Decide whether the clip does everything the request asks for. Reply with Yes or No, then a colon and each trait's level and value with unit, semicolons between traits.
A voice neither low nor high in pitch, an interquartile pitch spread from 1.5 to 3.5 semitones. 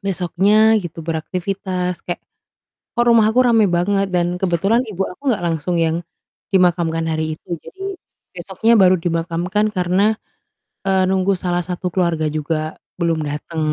Yes: medium, 180 Hz; average, 3.0 semitones